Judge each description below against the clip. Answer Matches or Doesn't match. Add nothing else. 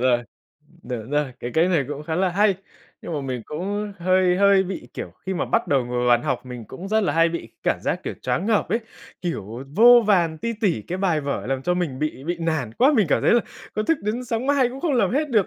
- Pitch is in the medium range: Matches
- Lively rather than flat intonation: Matches